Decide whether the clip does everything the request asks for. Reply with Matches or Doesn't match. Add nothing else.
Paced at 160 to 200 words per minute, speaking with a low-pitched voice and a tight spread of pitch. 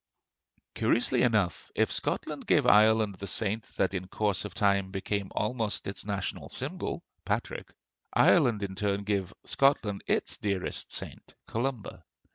Doesn't match